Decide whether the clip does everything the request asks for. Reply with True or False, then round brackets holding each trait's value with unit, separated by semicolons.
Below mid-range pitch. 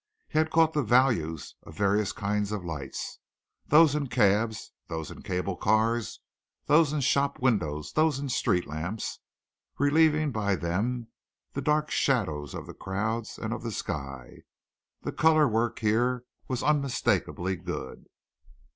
True (115 Hz)